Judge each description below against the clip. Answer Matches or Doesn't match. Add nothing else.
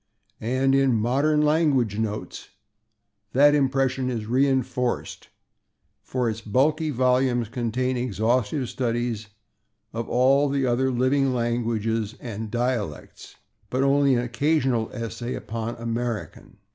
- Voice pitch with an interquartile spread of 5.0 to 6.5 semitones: Doesn't match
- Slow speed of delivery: Matches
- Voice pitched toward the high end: Doesn't match